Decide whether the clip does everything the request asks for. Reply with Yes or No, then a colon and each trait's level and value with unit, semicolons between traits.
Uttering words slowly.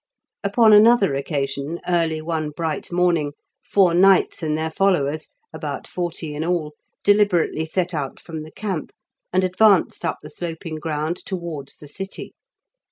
No: average, 145 wpm